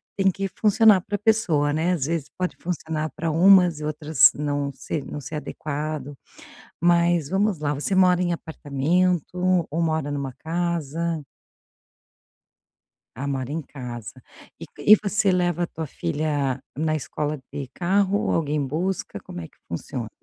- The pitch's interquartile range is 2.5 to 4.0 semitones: Yes, average, 3.7 semitones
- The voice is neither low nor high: Yes, medium, 160 Hz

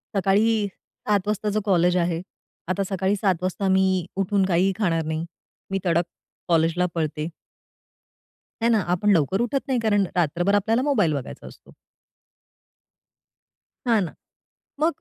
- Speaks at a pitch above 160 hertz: Yes, high, 190 Hz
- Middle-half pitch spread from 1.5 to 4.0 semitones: Yes, average, 3.3 semitones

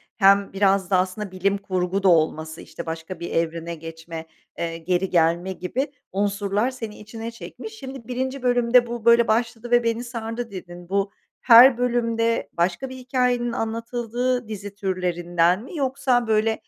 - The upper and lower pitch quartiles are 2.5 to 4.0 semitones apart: No, average, 4.8 semitones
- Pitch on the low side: No, high, 215 Hz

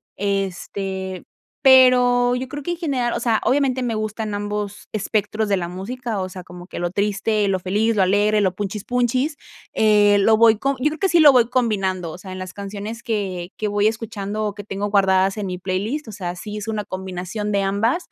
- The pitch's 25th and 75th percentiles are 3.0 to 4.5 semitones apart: Yes, average, 3.3 semitones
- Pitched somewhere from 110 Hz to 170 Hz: No, high, 210 Hz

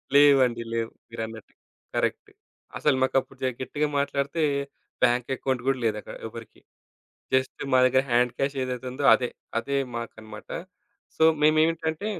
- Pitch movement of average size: Yes, average, 3.2 semitones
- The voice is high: No, low, 130 Hz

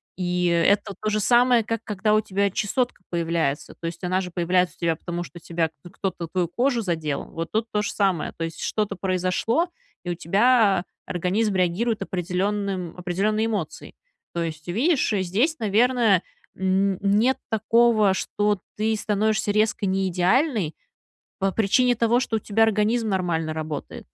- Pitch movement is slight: No, average, 3.8 semitones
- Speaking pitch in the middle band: No, high, 195 Hz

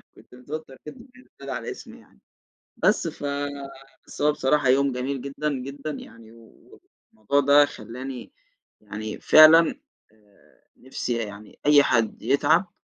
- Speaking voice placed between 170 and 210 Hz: No, low, 135 Hz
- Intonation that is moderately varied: Yes, average, 4.0 semitones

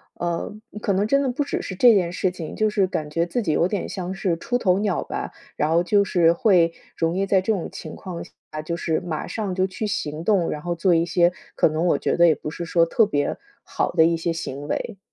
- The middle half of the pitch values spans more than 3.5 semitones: No, average, 3.0 semitones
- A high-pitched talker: No, medium, 175 Hz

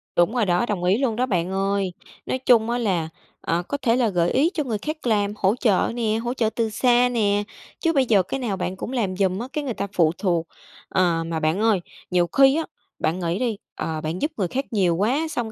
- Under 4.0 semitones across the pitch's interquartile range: No, average, 5.3 semitones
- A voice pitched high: Yes, high, 210 Hz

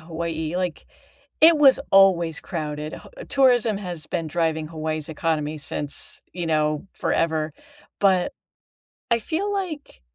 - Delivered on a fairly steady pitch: No, average, 4.7 semitones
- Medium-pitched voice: Yes, medium, 165 Hz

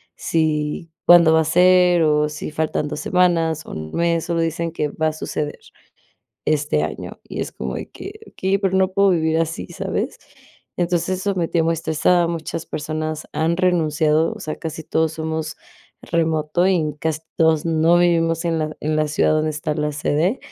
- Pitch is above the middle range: No, medium, 160 Hz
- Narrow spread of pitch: Yes, narrow, 1.8 semitones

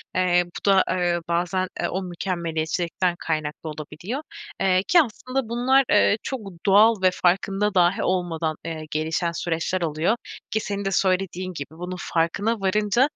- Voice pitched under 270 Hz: Yes, medium, 185 Hz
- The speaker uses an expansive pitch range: No, average, 3.1 semitones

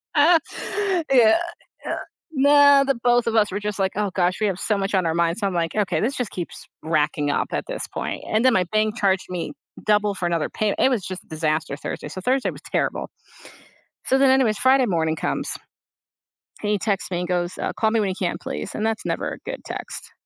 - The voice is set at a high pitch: Yes, high, 205 Hz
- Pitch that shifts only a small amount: No, wide, 5.4 semitones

